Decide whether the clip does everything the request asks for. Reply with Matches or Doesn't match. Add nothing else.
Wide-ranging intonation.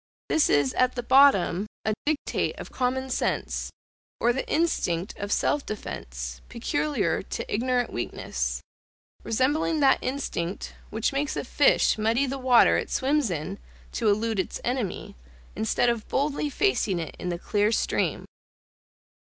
Matches